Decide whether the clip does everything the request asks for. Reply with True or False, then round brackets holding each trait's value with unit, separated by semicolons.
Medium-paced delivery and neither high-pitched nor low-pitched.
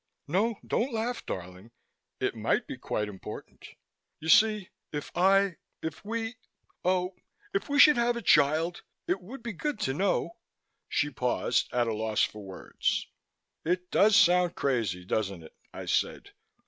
True (160 wpm; 180 Hz)